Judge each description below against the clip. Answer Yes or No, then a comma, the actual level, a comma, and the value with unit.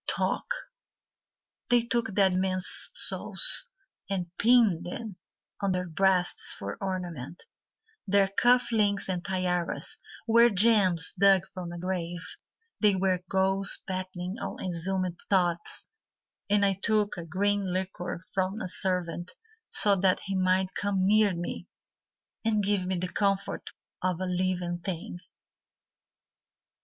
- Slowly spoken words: Yes, slow, 125 wpm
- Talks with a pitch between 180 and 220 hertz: Yes, high, 190 Hz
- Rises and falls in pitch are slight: Yes, narrow, 2.1 semitones